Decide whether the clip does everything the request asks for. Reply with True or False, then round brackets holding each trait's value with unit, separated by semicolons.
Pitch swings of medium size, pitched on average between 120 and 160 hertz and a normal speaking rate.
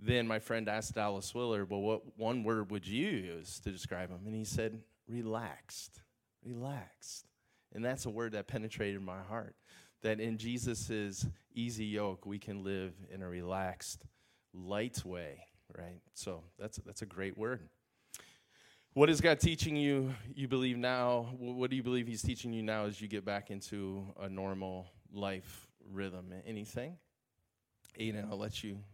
False (3.3 semitones; 110 Hz; 165 wpm)